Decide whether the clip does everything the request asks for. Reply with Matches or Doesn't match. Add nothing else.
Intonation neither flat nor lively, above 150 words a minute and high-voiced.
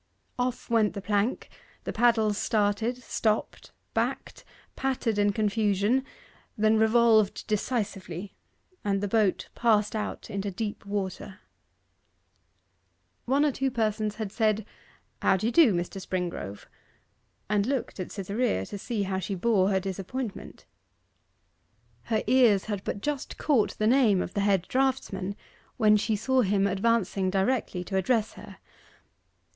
Doesn't match